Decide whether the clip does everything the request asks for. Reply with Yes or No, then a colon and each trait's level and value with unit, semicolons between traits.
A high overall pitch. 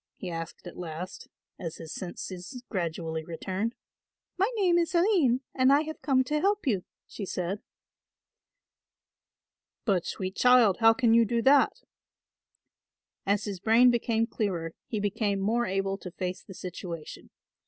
Yes: high, 205 Hz